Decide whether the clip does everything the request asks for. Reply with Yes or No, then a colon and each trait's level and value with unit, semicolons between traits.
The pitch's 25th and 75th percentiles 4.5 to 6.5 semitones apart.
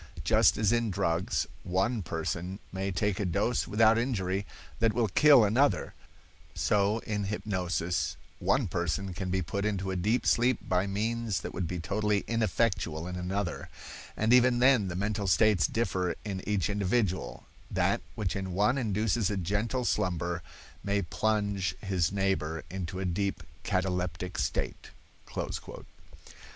No: average, 3.1 semitones